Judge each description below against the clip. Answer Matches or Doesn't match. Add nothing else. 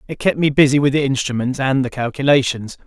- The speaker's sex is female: Doesn't match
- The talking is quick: Matches